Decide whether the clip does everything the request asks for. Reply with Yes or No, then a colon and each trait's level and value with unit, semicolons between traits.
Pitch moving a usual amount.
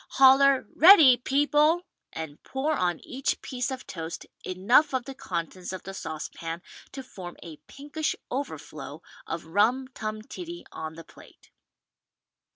No: wide, 7.9 semitones